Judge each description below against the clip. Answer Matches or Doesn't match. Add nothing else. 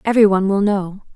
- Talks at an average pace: Doesn't match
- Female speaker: Matches